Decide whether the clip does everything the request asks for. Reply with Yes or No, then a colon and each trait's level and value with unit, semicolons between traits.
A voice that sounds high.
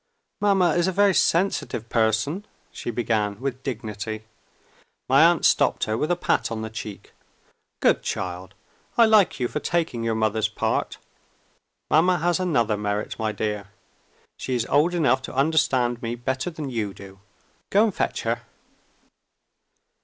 No: low, 120 Hz